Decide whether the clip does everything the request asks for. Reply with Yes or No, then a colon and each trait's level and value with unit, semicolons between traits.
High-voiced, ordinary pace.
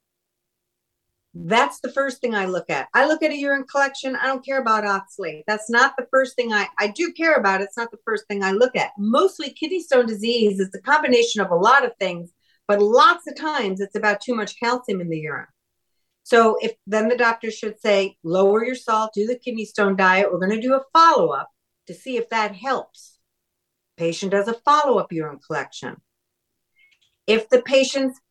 No: high, 230 Hz; fast, 210 wpm